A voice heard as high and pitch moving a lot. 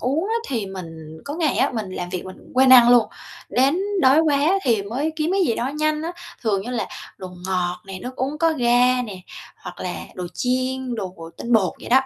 Yes: high, 245 Hz; wide, 6.6 semitones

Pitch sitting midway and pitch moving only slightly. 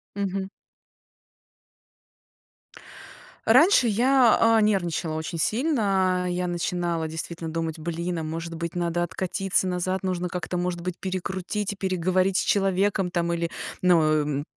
Yes: medium, 180 Hz; narrow, 2.3 semitones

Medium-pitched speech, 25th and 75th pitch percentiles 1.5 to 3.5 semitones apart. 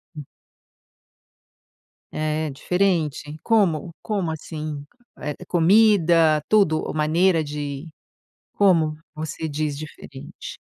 Yes: medium, 155 Hz; average, 2.8 semitones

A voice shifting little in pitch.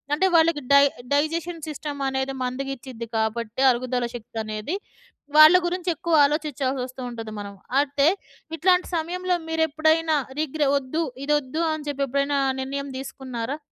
No: average, 3.7 semitones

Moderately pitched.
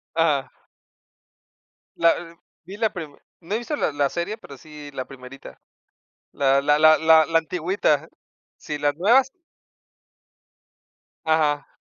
Yes: medium, 155 Hz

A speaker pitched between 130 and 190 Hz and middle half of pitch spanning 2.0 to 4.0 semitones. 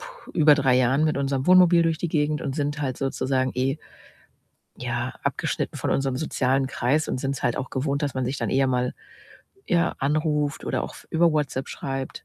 Yes: medium, 140 Hz; average, 2.7 semitones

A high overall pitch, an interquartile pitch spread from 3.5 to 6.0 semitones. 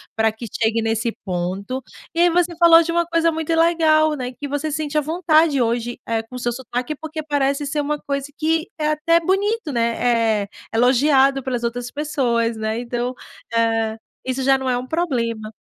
Yes: very high, 270 Hz; average, 5.0 semitones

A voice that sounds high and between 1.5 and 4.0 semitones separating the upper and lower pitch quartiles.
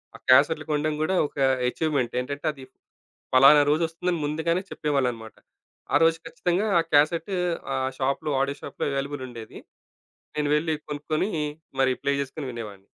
No: medium, 145 Hz; average, 3.4 semitones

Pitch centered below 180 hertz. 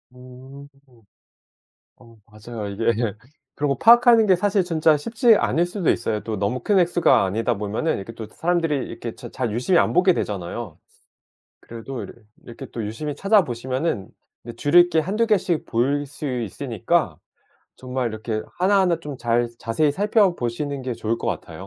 Yes: low, 135 Hz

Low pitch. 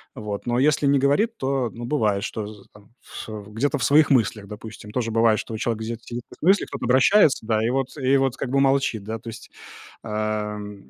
Yes: low, 115 Hz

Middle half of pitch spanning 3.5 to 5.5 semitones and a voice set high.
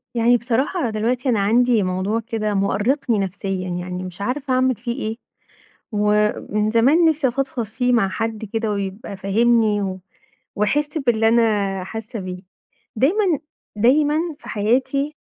Yes: average, 3.8 semitones; high, 225 Hz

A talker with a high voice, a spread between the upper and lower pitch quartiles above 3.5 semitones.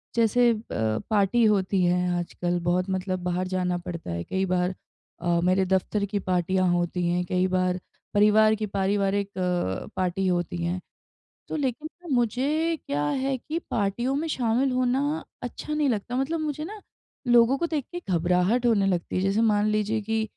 Yes: high, 195 Hz; average, 4.9 semitones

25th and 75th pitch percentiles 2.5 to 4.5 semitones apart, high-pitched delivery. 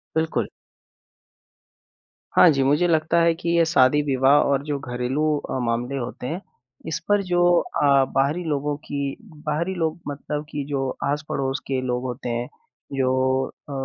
No: average, 3.3 semitones; medium, 140 Hz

